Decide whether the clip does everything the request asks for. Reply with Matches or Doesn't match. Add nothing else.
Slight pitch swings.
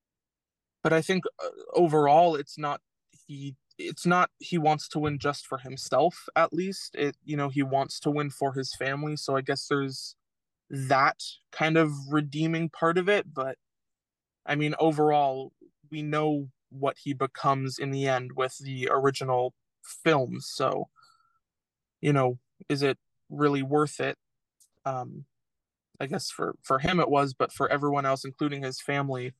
Matches